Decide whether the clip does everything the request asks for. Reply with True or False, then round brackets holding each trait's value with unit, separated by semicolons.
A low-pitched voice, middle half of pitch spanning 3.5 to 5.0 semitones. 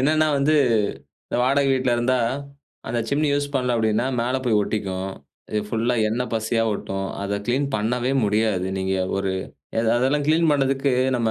True (120 Hz; 4.1 semitones)